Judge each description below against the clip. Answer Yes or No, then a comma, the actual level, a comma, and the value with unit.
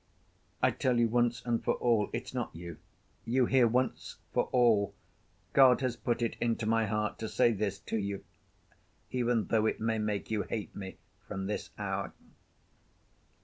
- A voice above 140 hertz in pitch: No, low, 115 Hz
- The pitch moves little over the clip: Yes, narrow, 2.2 semitones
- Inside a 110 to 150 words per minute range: No, average, 170 wpm